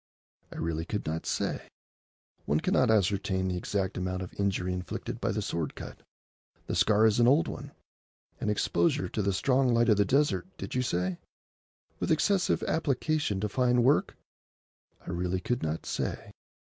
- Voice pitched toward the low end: Yes, low, 105 Hz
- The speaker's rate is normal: Yes, average, 160 wpm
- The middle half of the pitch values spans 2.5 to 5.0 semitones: No, wide, 5.6 semitones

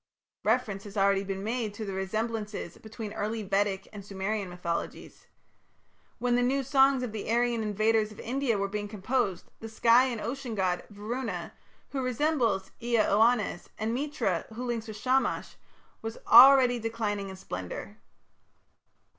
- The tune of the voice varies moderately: Yes, average, 3.5 semitones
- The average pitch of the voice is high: Yes, high, 220 Hz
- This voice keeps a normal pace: Yes, average, 150 wpm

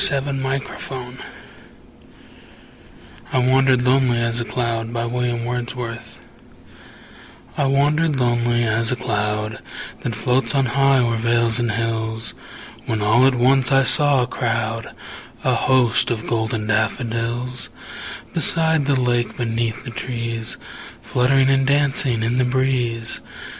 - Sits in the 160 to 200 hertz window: No, low, 120 Hz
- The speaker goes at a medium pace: No, slow, 120 wpm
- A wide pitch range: No, narrow, 2.4 semitones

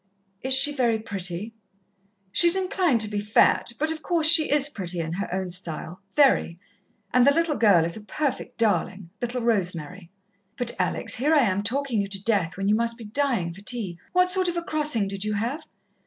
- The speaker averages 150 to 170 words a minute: No, average, 200 wpm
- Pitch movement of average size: No, wide, 6.9 semitones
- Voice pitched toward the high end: Yes, high, 225 Hz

